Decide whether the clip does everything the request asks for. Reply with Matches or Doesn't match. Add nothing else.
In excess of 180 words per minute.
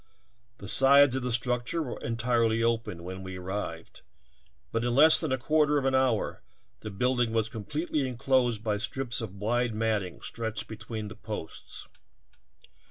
Doesn't match